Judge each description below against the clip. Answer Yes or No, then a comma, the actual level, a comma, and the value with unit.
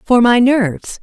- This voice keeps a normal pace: Yes, average, 175 wpm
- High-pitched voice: Yes, high, 235 Hz